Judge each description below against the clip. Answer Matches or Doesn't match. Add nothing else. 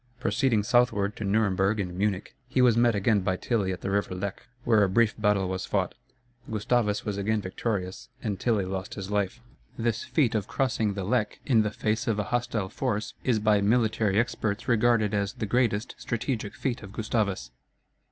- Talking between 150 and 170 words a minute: Doesn't match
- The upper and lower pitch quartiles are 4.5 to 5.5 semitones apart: Doesn't match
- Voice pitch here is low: Matches